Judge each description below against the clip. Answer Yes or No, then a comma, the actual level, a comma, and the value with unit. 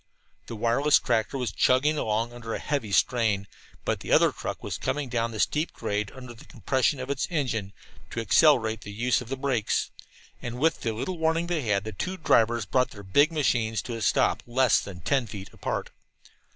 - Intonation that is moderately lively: Yes, average, 4.1 semitones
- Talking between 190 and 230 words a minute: Yes, average, 200 wpm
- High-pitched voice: No, low, 120 Hz